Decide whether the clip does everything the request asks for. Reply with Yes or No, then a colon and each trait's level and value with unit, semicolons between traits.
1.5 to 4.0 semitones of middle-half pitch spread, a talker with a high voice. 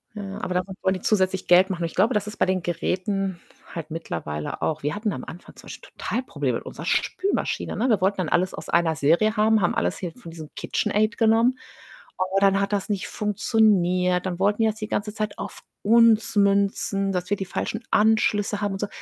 Yes: average, 2.9 semitones; high, 195 Hz